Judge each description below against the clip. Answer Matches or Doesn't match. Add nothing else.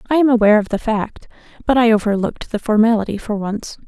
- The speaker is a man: Doesn't match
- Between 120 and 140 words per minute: Doesn't match